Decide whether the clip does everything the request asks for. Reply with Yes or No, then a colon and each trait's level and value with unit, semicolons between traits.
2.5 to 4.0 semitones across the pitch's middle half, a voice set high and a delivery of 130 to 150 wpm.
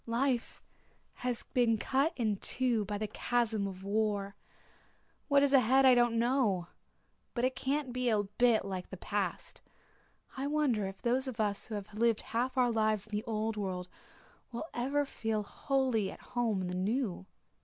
No: average, 3.6 semitones; high, 230 Hz; average, 175 wpm